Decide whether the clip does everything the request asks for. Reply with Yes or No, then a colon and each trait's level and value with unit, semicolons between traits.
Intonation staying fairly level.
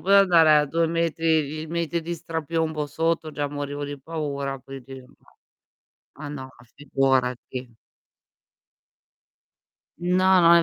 No: average, 3.1 semitones